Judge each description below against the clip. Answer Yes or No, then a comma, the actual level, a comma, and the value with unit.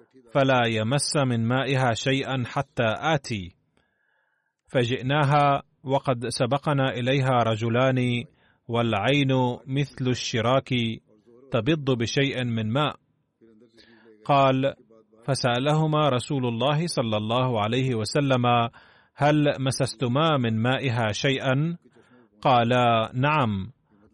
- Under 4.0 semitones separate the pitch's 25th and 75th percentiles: Yes, average, 3.1 semitones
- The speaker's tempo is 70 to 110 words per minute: Yes, average, 85 wpm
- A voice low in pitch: Yes, low, 130 Hz